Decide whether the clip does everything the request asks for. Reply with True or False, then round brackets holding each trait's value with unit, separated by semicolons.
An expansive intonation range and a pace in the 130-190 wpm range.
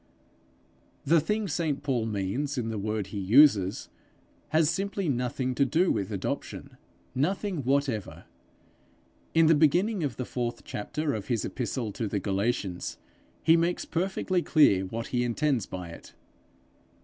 True (6.7 semitones; 145 wpm)